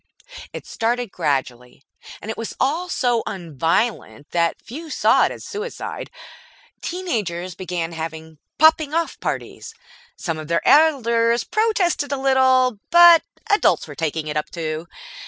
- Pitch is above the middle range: Yes, high, 230 Hz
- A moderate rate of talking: Yes, average, 145 wpm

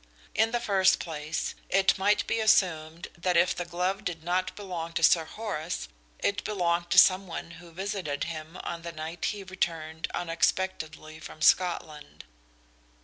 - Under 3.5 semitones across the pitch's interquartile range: Yes, average, 2.8 semitones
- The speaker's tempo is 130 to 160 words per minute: Yes, average, 155 wpm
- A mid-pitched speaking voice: Yes, medium, 175 Hz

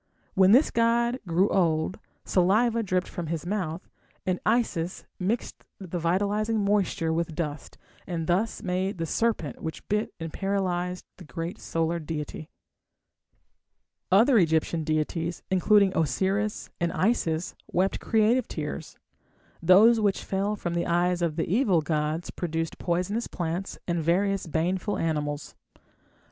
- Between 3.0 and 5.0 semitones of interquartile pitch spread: Yes, average, 3.6 semitones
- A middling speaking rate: No, slow, 130 wpm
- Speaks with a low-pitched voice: No, medium, 180 Hz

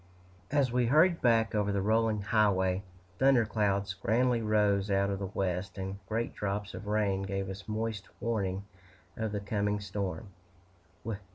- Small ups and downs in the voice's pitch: Yes, narrow, 2.3 semitones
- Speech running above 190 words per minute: No, average, 155 wpm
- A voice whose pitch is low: Yes, low, 105 Hz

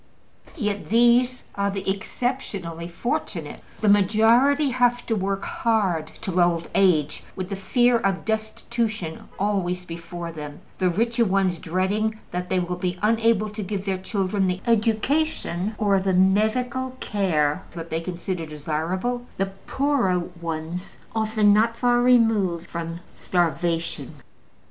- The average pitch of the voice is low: No, high, 195 Hz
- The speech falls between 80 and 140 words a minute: Yes, slow, 135 wpm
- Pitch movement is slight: No, average, 4.3 semitones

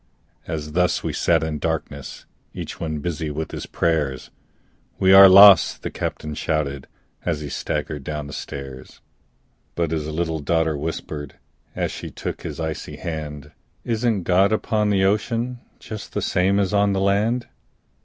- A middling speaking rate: Yes, average, 155 wpm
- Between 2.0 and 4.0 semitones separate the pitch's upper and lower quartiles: No, average, 4.6 semitones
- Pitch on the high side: No, very low, 80 Hz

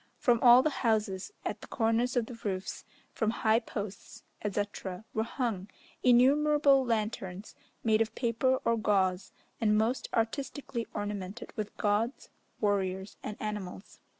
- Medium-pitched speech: No, high, 220 Hz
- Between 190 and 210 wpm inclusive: No, slow, 135 wpm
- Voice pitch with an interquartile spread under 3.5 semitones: Yes, average, 2.8 semitones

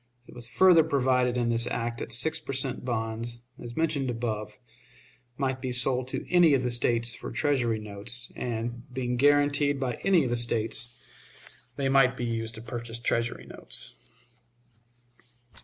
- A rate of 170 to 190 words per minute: No, average, 160 wpm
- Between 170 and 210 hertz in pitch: No, low, 125 Hz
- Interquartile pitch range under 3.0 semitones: Yes, narrow, 2.4 semitones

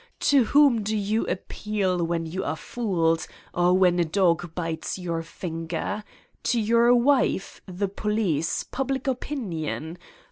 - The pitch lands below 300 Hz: Yes, high, 190 Hz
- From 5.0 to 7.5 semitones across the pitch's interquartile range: Yes, wide, 5.4 semitones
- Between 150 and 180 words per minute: No, slow, 135 wpm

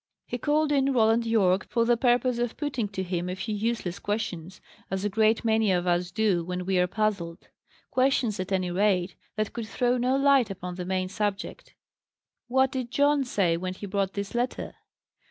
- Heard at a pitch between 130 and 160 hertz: No, high, 210 Hz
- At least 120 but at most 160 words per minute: No, average, 190 wpm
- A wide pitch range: No, average, 4.6 semitones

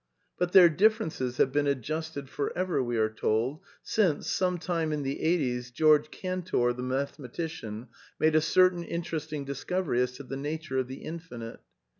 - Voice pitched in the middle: Yes, medium, 150 Hz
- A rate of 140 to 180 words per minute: Yes, average, 170 wpm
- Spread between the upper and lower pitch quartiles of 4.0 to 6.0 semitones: Yes, average, 4.9 semitones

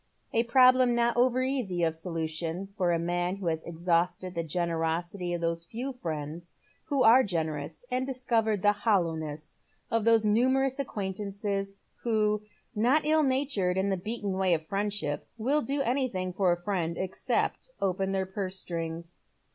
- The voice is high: Yes, high, 195 Hz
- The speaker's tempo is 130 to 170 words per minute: Yes, average, 155 wpm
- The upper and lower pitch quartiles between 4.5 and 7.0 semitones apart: Yes, wide, 5.5 semitones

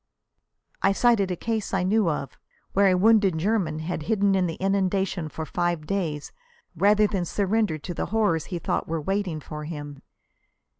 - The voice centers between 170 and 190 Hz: Yes, medium, 185 Hz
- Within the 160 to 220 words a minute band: Yes, average, 170 wpm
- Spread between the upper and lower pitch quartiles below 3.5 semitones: No, average, 4.1 semitones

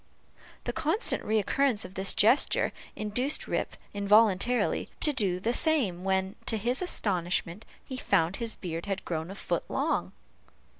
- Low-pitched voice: No, high, 205 Hz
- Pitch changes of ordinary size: Yes, average, 4.6 semitones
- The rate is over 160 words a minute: No, average, 145 wpm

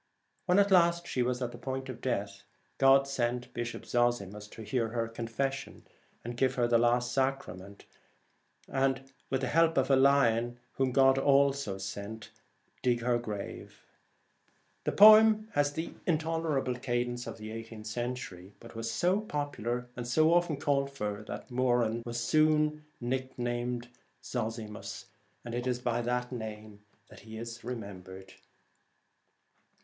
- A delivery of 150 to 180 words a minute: No, average, 140 wpm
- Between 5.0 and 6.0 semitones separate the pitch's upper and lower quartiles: No, average, 3.0 semitones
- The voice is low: Yes, low, 125 Hz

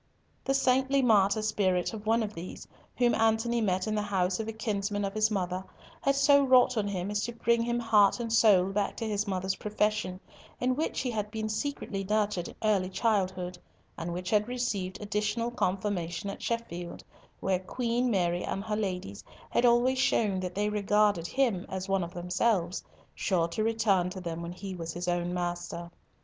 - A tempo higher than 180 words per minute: Yes, average, 190 wpm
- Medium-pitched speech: No, high, 205 Hz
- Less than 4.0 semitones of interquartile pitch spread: Yes, average, 3.6 semitones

